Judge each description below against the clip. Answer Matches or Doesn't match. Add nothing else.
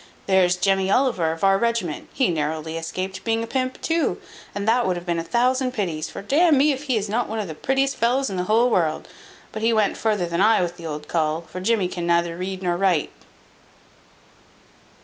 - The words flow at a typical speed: Doesn't match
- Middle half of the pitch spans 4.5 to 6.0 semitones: Matches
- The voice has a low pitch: Doesn't match